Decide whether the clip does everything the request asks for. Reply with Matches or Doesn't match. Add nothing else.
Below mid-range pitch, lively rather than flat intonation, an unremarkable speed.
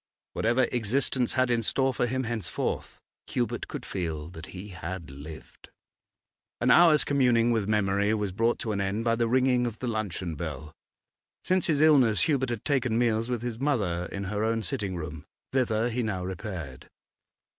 Doesn't match